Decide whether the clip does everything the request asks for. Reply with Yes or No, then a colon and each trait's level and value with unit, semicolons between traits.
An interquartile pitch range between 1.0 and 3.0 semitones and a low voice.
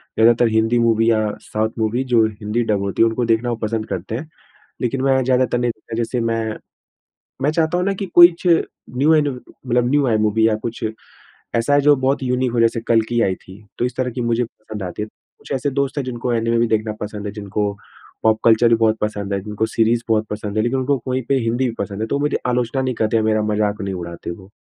Yes: average, 2.7 semitones; low, 115 Hz